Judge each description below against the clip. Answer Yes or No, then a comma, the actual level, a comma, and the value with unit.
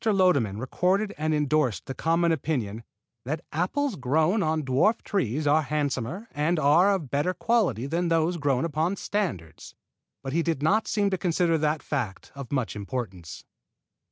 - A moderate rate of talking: Yes, average, 155 wpm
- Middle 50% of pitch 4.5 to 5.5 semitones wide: Yes, average, 5.1 semitones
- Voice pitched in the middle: Yes, medium, 155 Hz